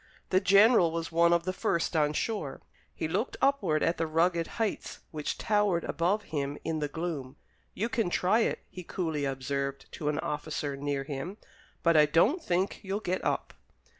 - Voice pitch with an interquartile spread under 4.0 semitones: No, average, 4.3 semitones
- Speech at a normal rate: Yes, average, 180 wpm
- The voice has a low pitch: No, medium, 165 Hz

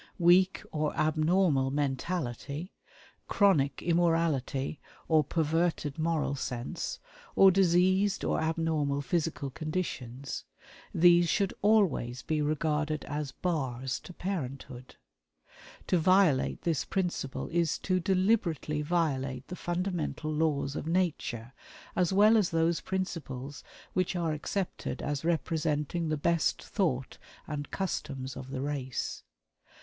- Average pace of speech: No, slow, 115 wpm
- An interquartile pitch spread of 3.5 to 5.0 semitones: Yes, average, 4.0 semitones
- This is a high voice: No, medium, 160 Hz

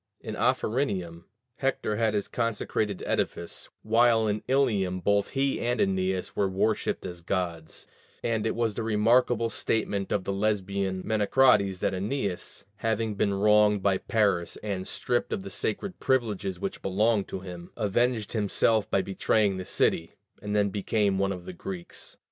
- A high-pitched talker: No, low, 105 Hz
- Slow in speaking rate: No, average, 155 wpm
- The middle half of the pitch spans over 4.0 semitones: No, average, 2.8 semitones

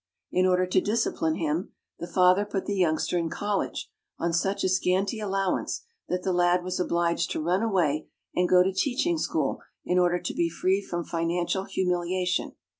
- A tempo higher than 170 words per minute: Yes, average, 180 wpm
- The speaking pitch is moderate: Yes, medium, 180 Hz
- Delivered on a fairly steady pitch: Yes, narrow, 1.9 semitones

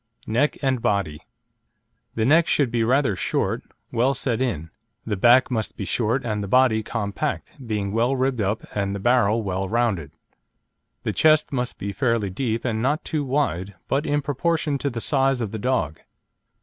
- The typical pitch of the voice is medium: No, low, 120 Hz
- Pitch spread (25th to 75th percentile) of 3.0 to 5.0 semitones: Yes, average, 4.6 semitones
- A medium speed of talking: Yes, average, 175 wpm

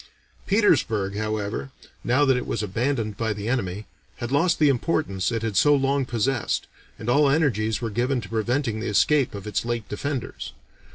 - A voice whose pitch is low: Yes, low, 120 Hz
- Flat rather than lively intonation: No, average, 4.3 semitones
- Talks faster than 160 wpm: Yes, average, 175 wpm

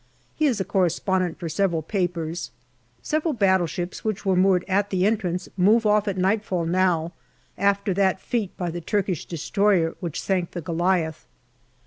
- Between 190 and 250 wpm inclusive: No, average, 155 wpm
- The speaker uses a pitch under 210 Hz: Yes, medium, 185 Hz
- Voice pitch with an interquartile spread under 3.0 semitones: Yes, narrow, 2.5 semitones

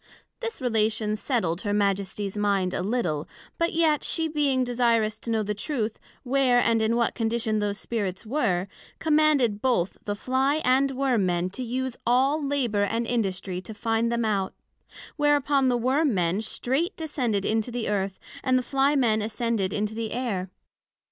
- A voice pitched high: Yes, high, 230 Hz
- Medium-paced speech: Yes, average, 170 wpm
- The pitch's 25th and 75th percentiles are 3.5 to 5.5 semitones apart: Yes, average, 4.1 semitones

